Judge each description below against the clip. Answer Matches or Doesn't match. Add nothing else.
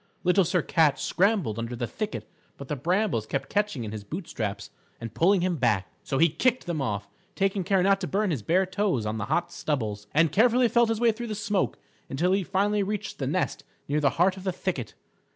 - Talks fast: Matches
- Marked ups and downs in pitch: Matches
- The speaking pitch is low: Doesn't match